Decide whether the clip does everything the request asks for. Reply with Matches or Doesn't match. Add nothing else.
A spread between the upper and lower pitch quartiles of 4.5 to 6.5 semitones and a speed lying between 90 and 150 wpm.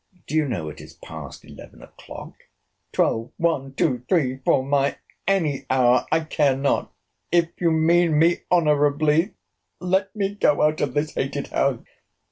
Doesn't match